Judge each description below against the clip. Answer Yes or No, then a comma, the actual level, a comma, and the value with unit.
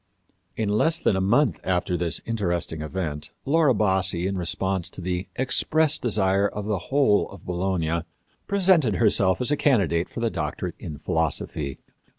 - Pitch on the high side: No, very low, 95 Hz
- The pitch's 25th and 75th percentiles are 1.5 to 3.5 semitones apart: No, average, 5.0 semitones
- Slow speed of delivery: No, average, 160 wpm